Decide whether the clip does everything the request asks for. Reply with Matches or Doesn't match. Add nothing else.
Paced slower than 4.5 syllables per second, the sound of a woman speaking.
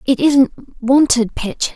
Matches